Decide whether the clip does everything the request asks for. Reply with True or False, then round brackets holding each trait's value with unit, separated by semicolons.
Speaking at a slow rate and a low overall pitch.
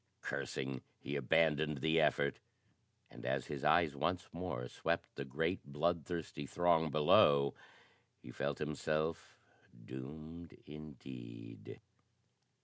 True (105 wpm; 75 Hz)